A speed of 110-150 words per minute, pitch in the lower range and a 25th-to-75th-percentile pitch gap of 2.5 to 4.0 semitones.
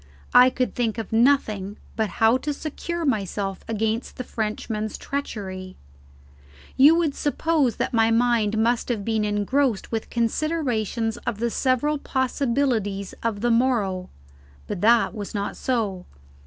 No: average, 140 wpm; high, 230 Hz; average, 3.5 semitones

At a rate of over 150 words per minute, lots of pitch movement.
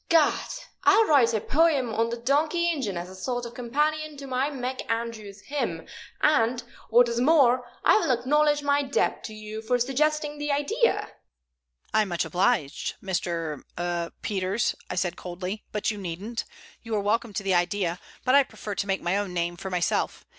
Yes: average, 180 wpm; wide, 6.6 semitones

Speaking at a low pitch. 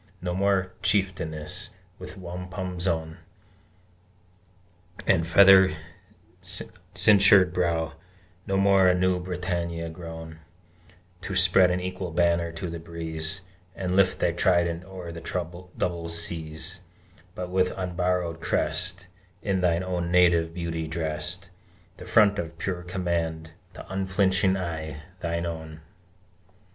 Yes: very low, 90 Hz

